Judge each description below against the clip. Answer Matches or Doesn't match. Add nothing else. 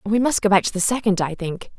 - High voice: Matches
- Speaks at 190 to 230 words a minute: Doesn't match